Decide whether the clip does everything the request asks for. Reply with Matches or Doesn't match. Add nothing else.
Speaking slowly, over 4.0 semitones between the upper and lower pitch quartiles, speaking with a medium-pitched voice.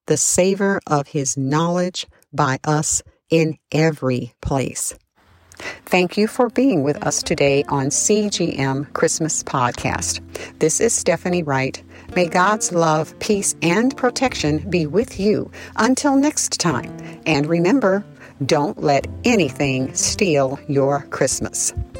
Matches